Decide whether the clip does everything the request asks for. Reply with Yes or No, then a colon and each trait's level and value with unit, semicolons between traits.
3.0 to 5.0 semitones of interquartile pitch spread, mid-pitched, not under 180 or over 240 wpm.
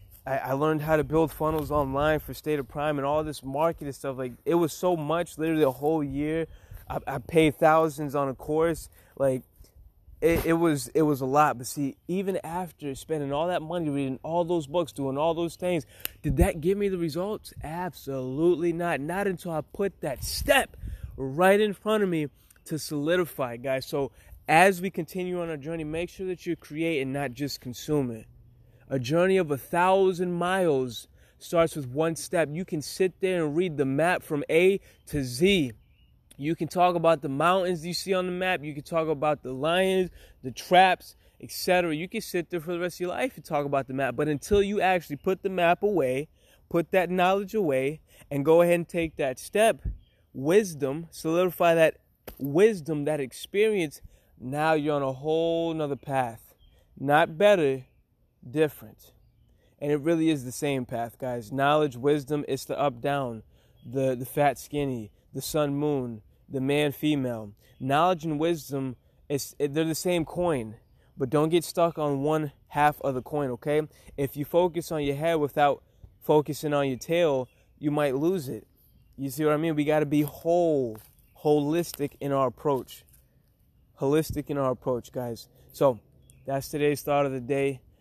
Yes: average, 4.0 semitones; medium, 150 Hz; average, 185 wpm